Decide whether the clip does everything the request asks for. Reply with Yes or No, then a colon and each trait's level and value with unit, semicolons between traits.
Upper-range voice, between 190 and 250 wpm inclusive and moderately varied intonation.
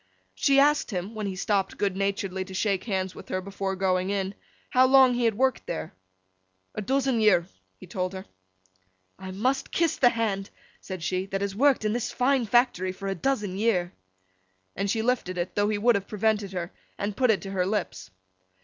Yes: high, 200 Hz; average, 200 wpm; average, 3.7 semitones